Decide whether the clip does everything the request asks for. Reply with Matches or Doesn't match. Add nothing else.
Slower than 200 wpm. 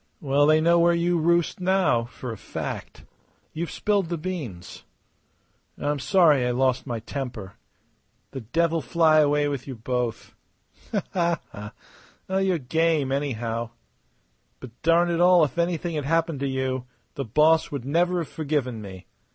Matches